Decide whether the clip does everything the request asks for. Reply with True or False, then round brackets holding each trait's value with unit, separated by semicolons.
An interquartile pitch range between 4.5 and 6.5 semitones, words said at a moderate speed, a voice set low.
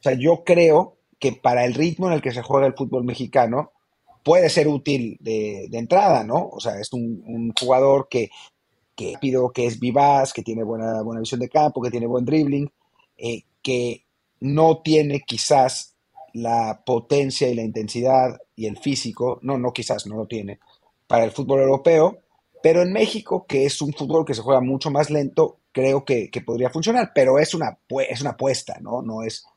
False (3.9 semitones; 195 wpm; 130 Hz)